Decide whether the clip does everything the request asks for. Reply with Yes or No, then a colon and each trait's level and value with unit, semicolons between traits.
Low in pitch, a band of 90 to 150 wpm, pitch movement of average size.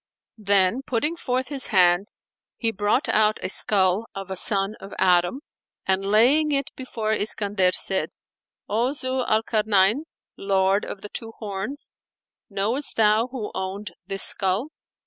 No: high, 210 Hz; average, 145 wpm; average, 4.0 semitones